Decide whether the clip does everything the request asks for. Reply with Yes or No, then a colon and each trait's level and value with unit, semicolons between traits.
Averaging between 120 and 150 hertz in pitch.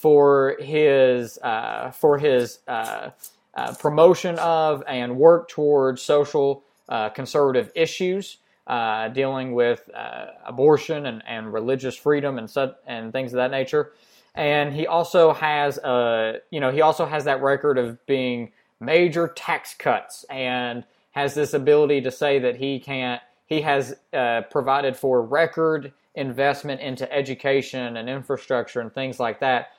Yes: medium, 140 Hz